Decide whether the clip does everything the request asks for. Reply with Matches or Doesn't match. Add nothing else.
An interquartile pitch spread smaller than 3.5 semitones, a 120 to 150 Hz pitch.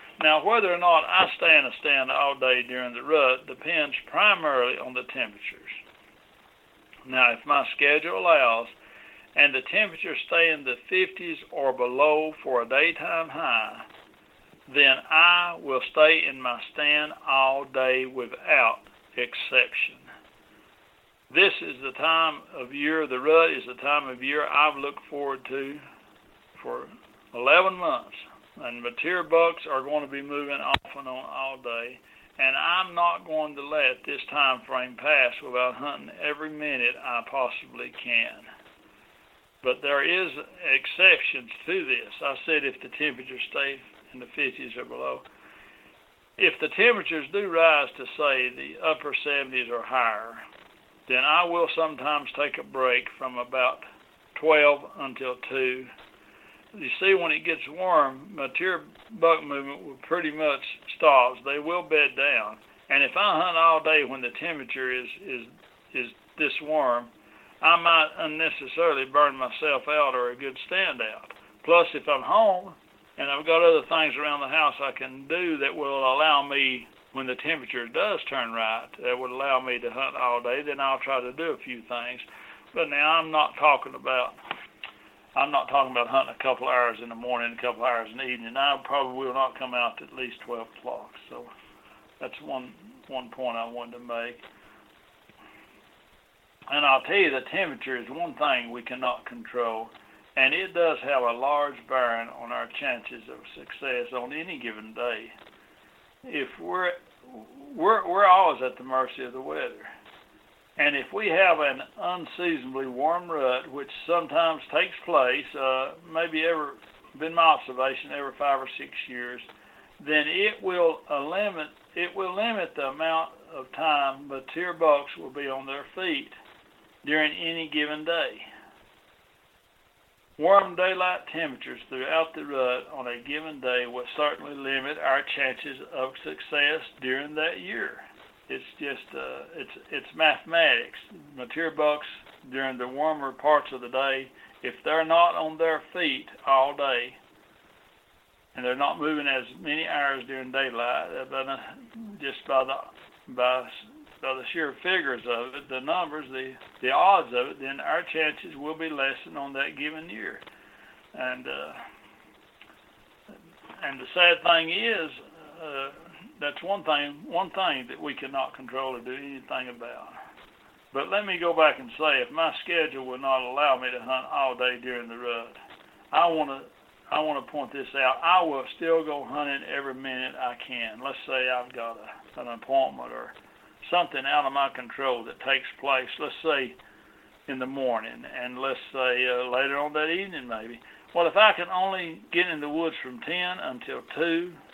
Doesn't match